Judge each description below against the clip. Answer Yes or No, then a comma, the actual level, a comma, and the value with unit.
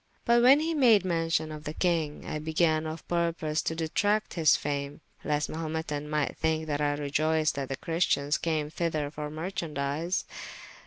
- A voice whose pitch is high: No, medium, 155 Hz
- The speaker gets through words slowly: No, average, 175 wpm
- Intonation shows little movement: Yes, narrow, 2.1 semitones